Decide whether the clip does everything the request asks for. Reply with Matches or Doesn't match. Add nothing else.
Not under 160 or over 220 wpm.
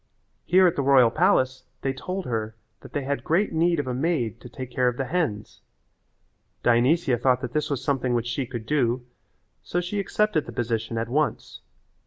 Matches